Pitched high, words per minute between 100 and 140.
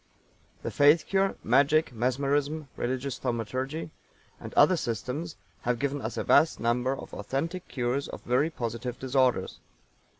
No: low, 135 Hz; slow, 135 wpm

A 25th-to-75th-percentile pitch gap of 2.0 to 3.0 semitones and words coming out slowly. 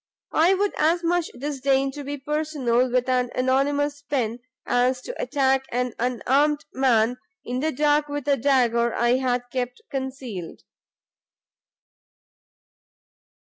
Yes: average, 2.7 semitones; slow, 125 wpm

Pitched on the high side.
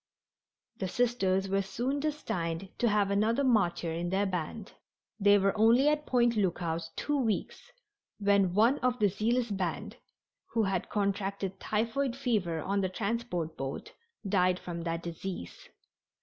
Yes: high, 200 Hz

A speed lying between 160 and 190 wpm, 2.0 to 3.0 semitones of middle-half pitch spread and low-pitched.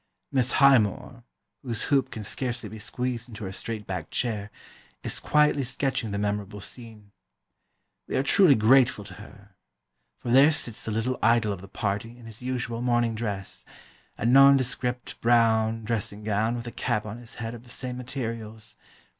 Yes: average, 170 wpm; average, 2.7 semitones; low, 115 Hz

